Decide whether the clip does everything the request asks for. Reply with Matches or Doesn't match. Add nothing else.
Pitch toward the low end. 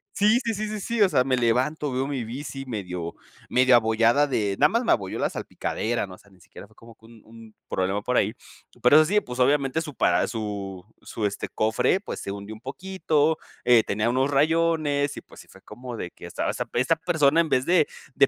Matches